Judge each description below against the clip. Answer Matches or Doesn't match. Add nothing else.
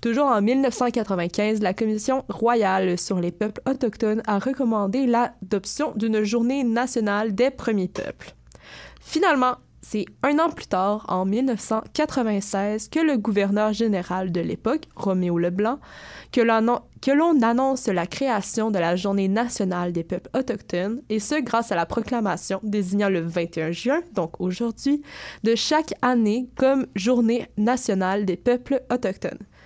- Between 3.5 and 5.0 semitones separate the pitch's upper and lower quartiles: Matches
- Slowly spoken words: Matches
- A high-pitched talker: Matches